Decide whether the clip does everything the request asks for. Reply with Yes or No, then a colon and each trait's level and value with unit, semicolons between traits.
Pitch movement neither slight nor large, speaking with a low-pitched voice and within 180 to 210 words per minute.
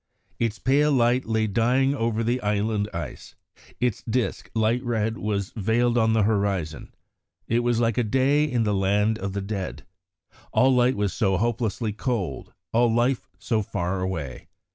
No: average, 3.1 semitones; low, 110 Hz; average, 165 wpm